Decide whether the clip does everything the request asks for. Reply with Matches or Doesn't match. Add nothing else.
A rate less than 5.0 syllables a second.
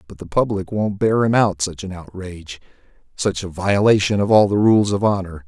Doesn't match